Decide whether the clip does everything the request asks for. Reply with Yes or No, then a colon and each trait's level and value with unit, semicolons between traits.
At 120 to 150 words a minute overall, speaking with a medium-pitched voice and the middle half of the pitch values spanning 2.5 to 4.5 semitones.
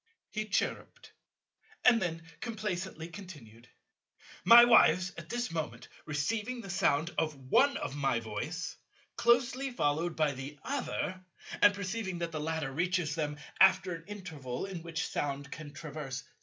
No: average, 145 wpm; medium, 170 Hz; wide, 5.4 semitones